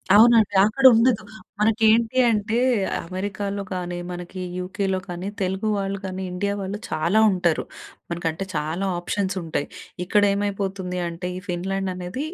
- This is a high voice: Yes, high, 195 Hz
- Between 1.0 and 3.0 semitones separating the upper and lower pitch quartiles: Yes, narrow, 2.4 semitones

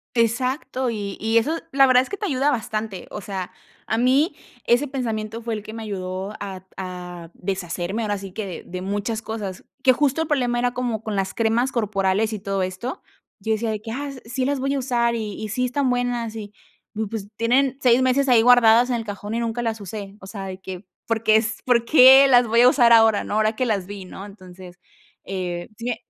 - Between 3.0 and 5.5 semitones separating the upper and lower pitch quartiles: Yes, average, 3.7 semitones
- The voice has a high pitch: Yes, high, 225 Hz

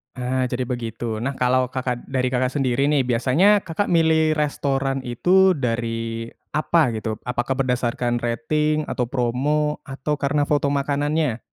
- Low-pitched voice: Yes, low, 130 Hz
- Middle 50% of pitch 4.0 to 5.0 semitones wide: No, average, 3.5 semitones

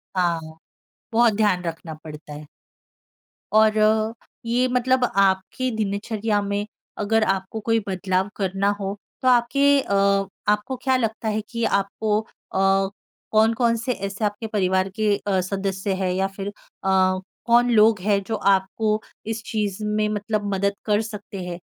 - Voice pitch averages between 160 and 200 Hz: No, high, 210 Hz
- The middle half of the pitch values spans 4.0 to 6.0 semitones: No, narrow, 2.4 semitones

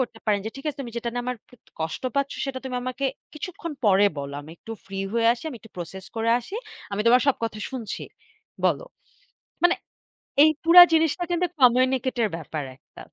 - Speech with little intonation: No, average, 4.7 semitones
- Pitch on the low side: No, high, 245 Hz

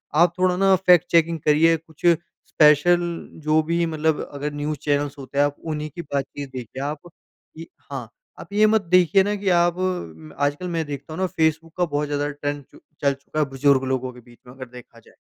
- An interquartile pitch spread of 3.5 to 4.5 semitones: No, average, 3.0 semitones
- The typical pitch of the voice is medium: Yes, medium, 150 Hz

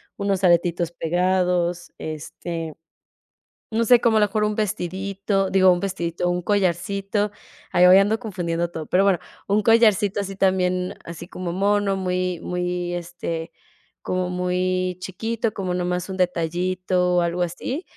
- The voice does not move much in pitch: Yes, narrow, 2.1 semitones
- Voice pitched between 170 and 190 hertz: Yes, medium, 185 Hz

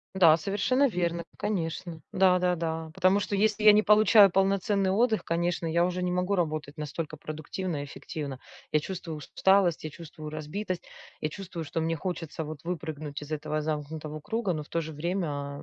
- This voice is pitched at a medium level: Yes, medium, 170 Hz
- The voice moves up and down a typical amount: Yes, average, 3.7 semitones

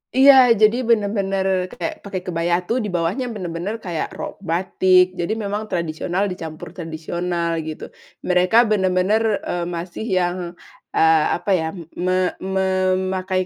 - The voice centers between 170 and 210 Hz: Yes, medium, 185 Hz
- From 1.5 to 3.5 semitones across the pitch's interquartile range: Yes, narrow, 2.4 semitones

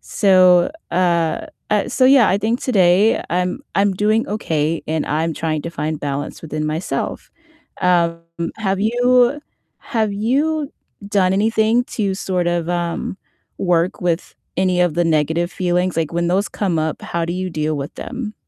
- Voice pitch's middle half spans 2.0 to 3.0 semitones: No, average, 4.1 semitones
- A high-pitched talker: No, medium, 180 Hz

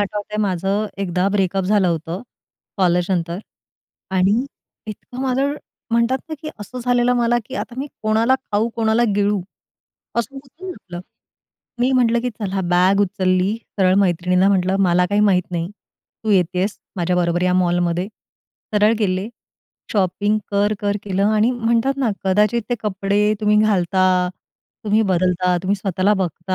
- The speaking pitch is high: Yes, high, 200 Hz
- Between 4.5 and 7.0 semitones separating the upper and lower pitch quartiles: No, average, 3.2 semitones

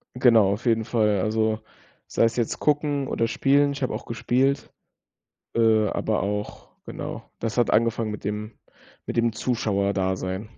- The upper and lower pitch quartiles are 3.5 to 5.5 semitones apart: No, average, 2.7 semitones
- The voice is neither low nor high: No, low, 115 Hz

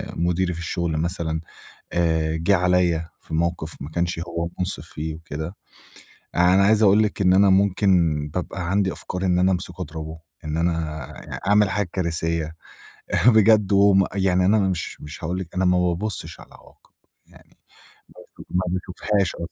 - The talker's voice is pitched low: Yes, very low, 90 Hz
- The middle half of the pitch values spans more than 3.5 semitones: No, narrow, 2.5 semitones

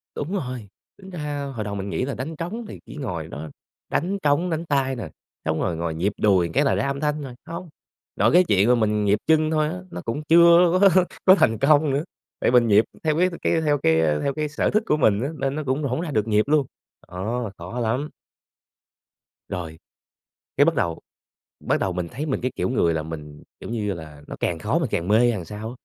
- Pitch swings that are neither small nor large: No, wide, 7.1 semitones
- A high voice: No, low, 130 Hz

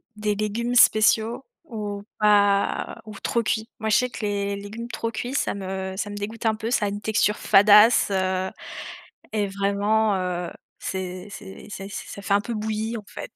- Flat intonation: Yes, narrow, 1.6 semitones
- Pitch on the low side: No, high, 210 Hz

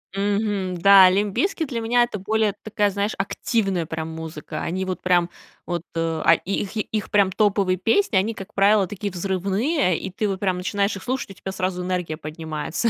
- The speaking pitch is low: No, high, 195 Hz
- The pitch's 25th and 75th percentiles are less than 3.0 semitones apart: Yes, narrow, 2.5 semitones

